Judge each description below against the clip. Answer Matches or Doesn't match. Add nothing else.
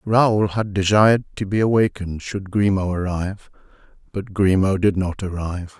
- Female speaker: Doesn't match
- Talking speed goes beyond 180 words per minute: Doesn't match